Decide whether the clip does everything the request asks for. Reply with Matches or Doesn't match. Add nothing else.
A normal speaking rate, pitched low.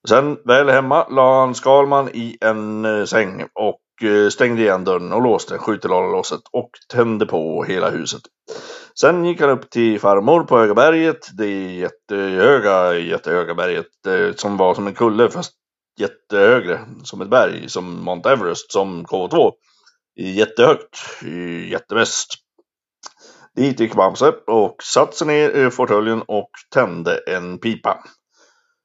Matches